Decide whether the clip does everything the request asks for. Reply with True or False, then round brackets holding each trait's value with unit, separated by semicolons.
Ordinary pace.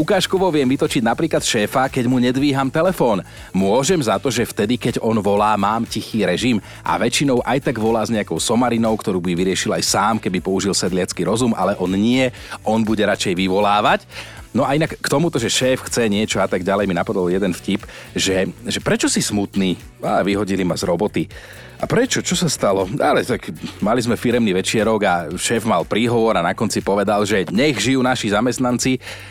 False (190 wpm)